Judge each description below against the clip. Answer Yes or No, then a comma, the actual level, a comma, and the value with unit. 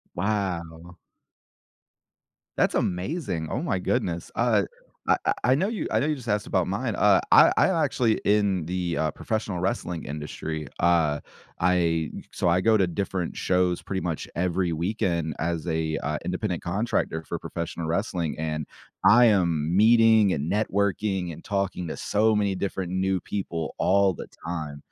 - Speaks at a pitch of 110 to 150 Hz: No, very low, 90 Hz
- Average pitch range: Yes, average, 3.6 semitones